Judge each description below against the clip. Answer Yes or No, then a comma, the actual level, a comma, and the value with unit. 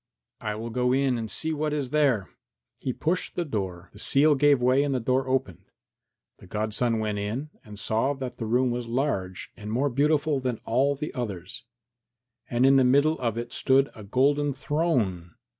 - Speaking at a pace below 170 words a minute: No, average, 190 wpm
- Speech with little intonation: No, average, 4.4 semitones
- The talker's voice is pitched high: No, low, 125 Hz